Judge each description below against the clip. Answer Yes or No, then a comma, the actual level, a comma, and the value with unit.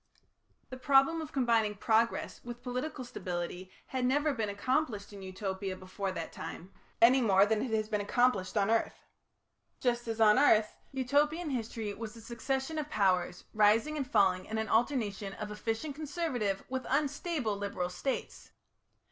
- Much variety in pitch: No, average, 4.6 semitones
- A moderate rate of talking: Yes, average, 155 wpm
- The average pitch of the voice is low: No, high, 225 Hz